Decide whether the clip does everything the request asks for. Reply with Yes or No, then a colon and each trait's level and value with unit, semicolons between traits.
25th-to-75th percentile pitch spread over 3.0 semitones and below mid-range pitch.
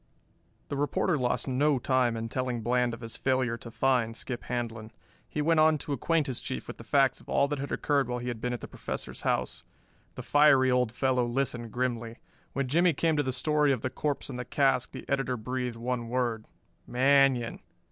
No: narrow, 2.6 semitones; low, 125 Hz